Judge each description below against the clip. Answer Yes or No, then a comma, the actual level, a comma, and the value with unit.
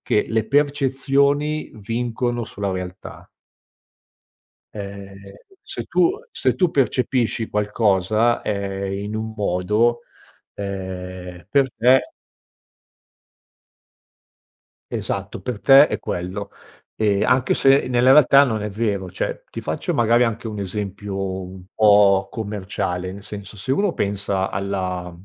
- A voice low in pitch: Yes, low, 105 Hz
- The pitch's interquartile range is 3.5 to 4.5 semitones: Yes, average, 3.8 semitones